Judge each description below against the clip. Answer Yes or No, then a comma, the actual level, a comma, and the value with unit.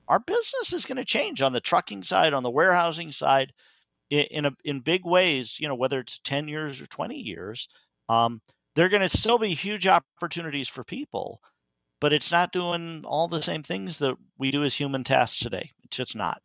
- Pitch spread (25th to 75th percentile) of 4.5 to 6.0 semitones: Yes, average, 4.8 semitones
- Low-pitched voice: No, medium, 155 Hz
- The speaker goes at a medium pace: No, fast, 210 wpm